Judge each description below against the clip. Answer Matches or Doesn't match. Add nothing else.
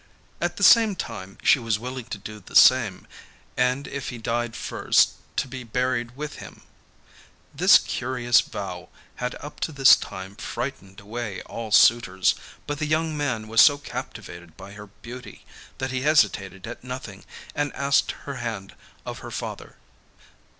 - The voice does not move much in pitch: Doesn't match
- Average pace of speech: Matches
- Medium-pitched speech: Doesn't match